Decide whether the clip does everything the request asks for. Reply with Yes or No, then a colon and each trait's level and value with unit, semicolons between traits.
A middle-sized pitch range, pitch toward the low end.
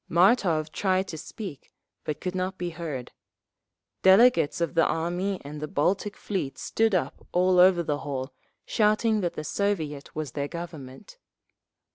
No: average, 4.1 semitones; medium, 175 Hz